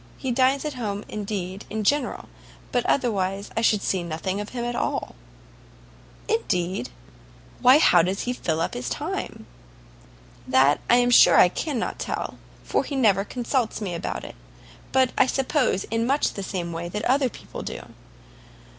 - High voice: Yes, high, 215 Hz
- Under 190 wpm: Yes, average, 165 wpm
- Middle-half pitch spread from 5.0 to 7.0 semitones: Yes, wide, 5.4 semitones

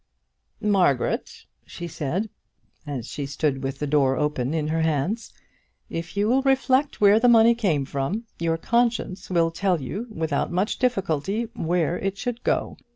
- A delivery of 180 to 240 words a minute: No, average, 160 wpm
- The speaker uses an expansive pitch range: Yes, wide, 6.9 semitones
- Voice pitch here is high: No, medium, 175 Hz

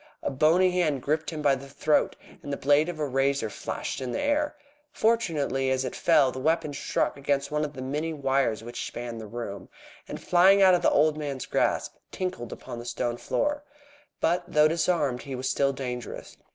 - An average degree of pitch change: Yes, average, 3.8 semitones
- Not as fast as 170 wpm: No, average, 200 wpm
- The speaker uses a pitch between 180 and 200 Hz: No, medium, 140 Hz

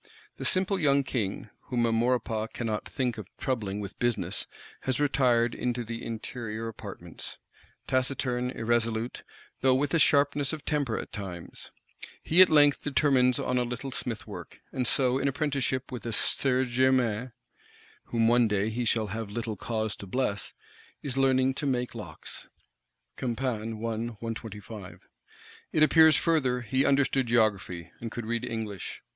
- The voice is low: Yes, low, 120 Hz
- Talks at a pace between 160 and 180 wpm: No, average, 145 wpm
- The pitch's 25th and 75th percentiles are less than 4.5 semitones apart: Yes, average, 3.0 semitones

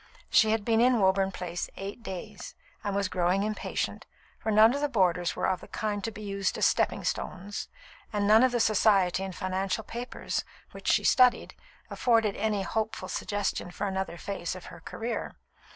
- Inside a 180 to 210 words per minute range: Yes, average, 185 wpm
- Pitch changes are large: No, average, 2.7 semitones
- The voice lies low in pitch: No, high, 205 Hz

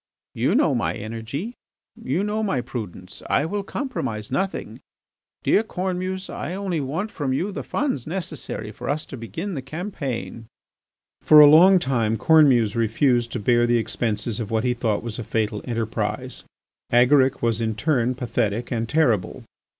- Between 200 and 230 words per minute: No, average, 160 wpm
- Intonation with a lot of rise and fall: Yes, wide, 6.2 semitones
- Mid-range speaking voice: No, low, 125 Hz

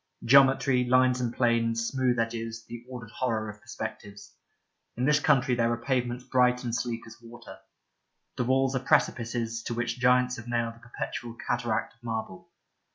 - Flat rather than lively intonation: Yes, narrow, 1.6 semitones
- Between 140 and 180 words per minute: Yes, average, 165 wpm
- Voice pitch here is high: No, low, 120 Hz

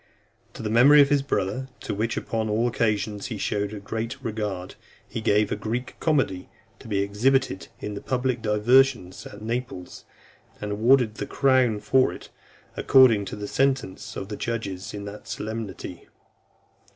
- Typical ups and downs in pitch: Yes, average, 3.7 semitones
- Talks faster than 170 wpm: No, average, 165 wpm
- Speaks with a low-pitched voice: Yes, low, 110 Hz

